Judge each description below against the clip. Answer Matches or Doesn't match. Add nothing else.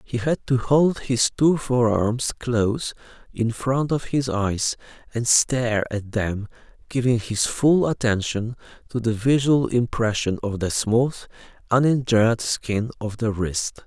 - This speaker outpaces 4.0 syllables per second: Doesn't match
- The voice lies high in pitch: Doesn't match